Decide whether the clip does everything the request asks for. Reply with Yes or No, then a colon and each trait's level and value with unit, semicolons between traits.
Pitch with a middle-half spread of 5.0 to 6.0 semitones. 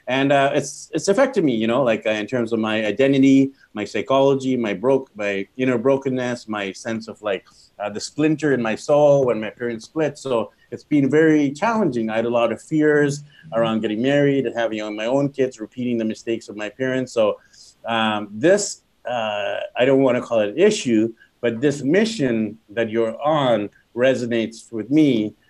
No: average, 4.1 semitones